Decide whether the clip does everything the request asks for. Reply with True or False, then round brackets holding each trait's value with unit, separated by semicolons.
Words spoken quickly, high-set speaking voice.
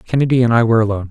False (270 wpm; 115 Hz)